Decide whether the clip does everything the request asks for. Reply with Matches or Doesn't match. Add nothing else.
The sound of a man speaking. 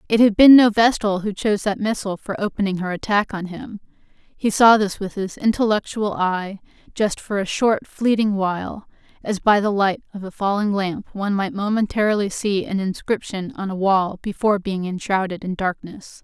Doesn't match